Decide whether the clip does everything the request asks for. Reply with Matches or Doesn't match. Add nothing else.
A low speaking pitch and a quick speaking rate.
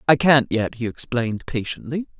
Doesn't match